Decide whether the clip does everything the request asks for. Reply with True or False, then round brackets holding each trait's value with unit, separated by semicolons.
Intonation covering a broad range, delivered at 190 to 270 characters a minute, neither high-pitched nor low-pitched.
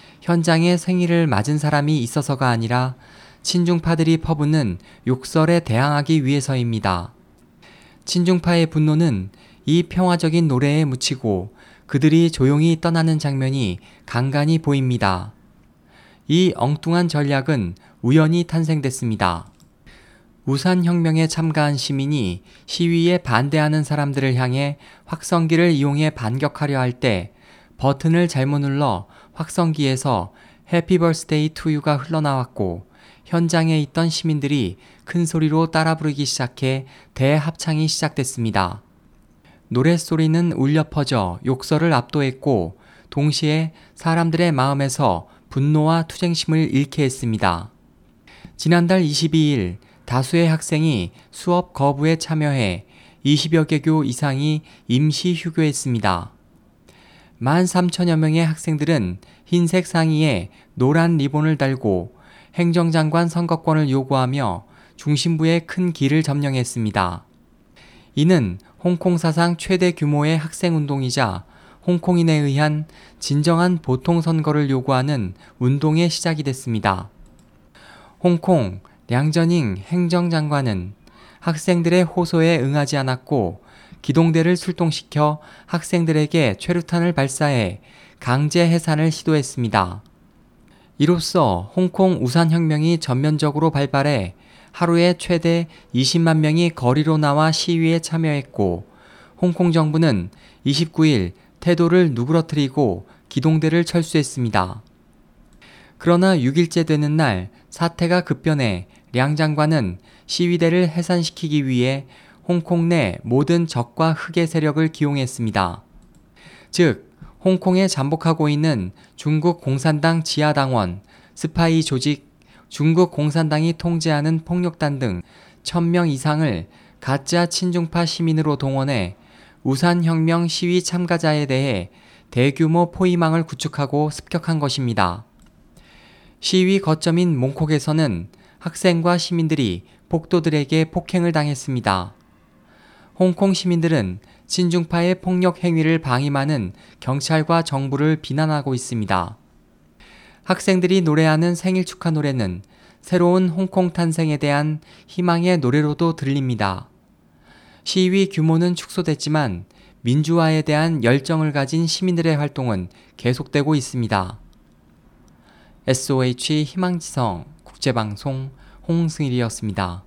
False (4.5 semitones; 265 characters per minute; 155 Hz)